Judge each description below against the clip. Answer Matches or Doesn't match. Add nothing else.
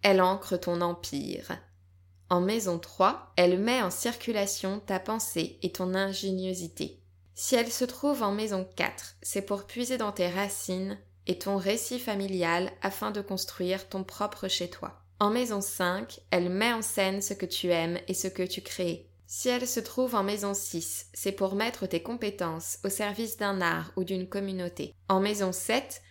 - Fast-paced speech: Doesn't match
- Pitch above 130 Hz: Matches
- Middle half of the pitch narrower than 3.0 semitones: Matches